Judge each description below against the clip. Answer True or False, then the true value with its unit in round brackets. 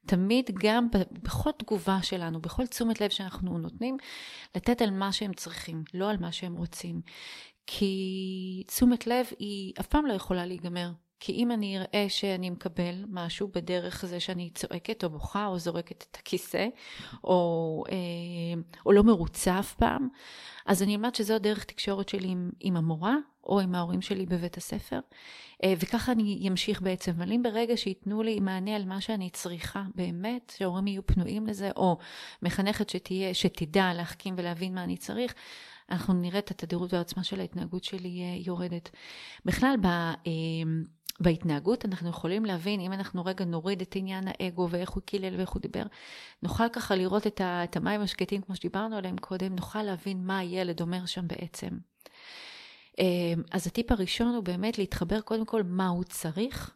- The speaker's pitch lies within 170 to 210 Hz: True (190 Hz)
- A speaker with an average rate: False (160 wpm)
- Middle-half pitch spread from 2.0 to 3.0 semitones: True (2.7 semitones)